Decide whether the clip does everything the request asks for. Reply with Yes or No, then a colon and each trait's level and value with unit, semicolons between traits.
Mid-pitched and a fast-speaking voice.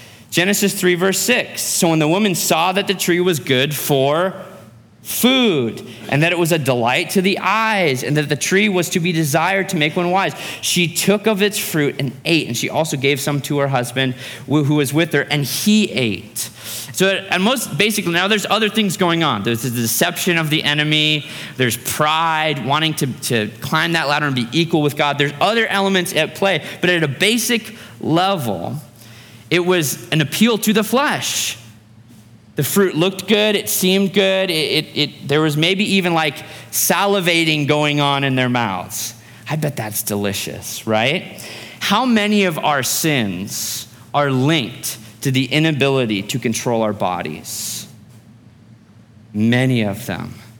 No: medium, 150 Hz; average, 175 wpm